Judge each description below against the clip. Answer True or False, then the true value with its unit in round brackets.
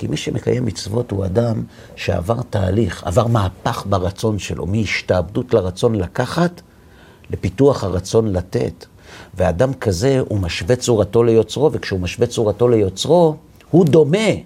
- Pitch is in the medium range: False (115 Hz)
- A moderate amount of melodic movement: True (4.3 semitones)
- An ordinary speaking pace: True (125 wpm)